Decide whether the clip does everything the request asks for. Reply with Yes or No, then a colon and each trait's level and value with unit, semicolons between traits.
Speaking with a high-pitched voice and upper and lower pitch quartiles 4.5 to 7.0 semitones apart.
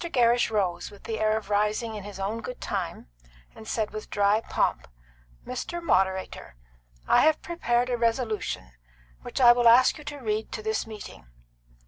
No: high, 220 Hz; average, 2.7 semitones